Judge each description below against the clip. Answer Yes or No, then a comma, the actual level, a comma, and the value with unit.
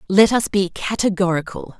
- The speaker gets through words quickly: No, slow, 135 wpm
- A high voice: Yes, high, 195 Hz